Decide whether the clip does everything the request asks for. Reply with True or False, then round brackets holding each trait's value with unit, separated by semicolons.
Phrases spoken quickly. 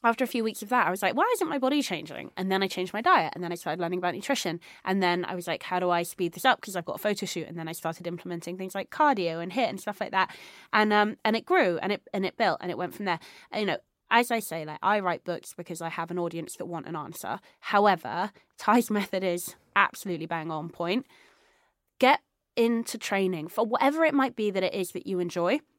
True (265 wpm)